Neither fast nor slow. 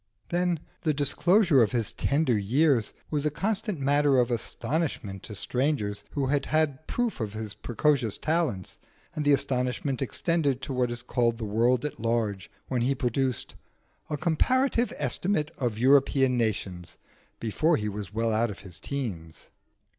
Yes: average, 155 wpm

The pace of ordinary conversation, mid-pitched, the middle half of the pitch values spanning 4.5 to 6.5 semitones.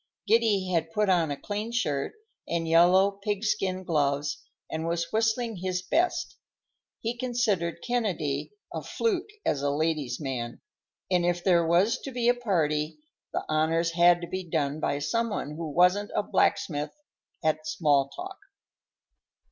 Yes: average, 155 wpm; medium, 175 Hz; average, 5.2 semitones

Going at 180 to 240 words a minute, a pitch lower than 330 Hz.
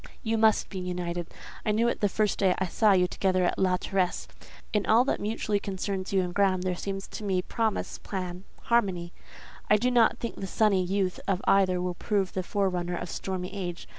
Yes: fast, 205 wpm; high, 190 Hz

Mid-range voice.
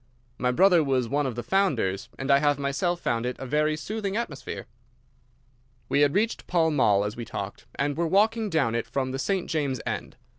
Yes: medium, 145 Hz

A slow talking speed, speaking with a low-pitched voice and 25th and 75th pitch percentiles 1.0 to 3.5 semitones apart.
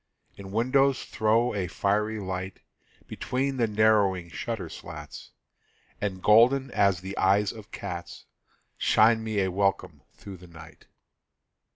Yes: slow, 130 wpm; low, 105 Hz; average, 2.9 semitones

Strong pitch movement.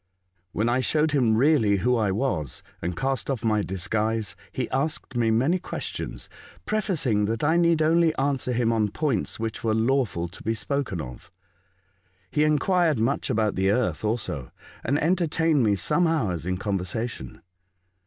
Yes: wide, 6.1 semitones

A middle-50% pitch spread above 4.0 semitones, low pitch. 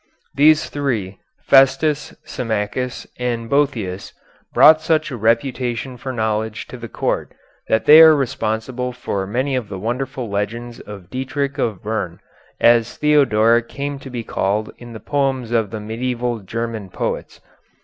No: average, 3.5 semitones; low, 120 Hz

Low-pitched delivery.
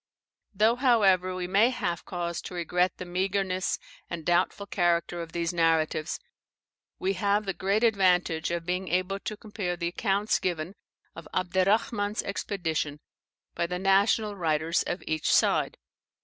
No: medium, 185 Hz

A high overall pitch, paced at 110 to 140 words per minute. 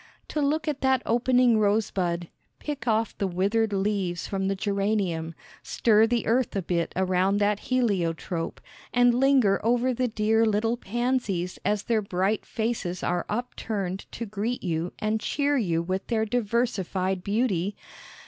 No: high, 210 Hz; average, 150 wpm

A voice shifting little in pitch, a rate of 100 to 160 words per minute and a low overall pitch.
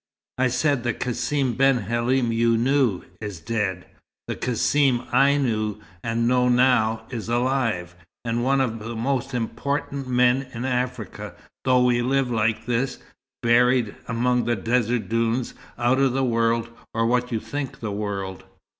Yes: narrow, 2.1 semitones; average, 155 wpm; low, 120 Hz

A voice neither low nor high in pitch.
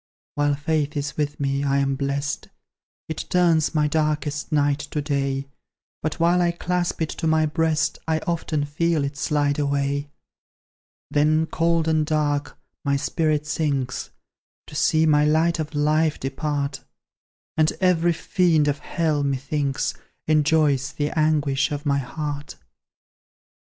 Yes: medium, 150 Hz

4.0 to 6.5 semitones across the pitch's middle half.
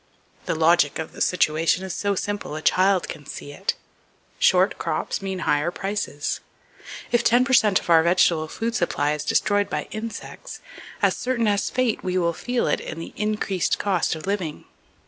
Yes: average, 4.5 semitones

